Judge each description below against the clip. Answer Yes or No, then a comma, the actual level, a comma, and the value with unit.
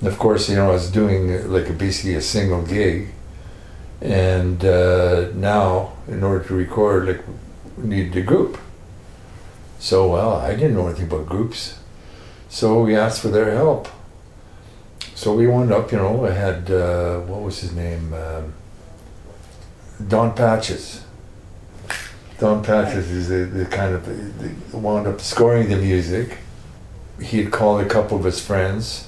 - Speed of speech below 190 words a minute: Yes, average, 155 wpm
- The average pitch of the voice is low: Yes, very low, 95 Hz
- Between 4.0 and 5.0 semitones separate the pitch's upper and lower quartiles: No, average, 2.8 semitones